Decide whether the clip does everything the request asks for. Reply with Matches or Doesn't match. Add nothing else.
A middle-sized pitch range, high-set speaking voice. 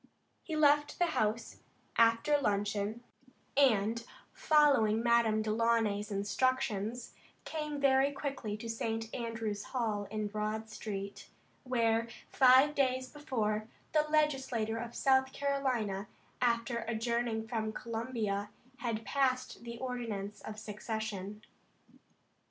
Matches